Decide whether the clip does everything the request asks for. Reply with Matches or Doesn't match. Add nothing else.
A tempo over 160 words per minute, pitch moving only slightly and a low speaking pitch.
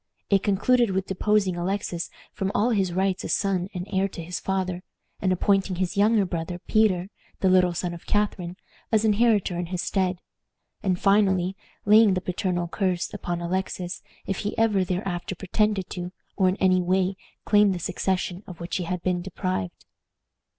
Doesn't match